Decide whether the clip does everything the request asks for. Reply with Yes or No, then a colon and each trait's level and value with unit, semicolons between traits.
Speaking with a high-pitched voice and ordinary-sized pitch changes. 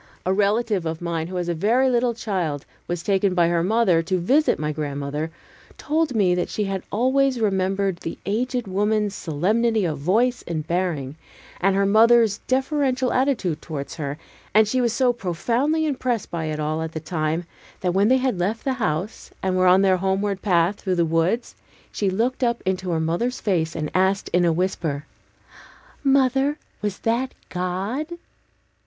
No: high, 195 Hz; wide, 5.7 semitones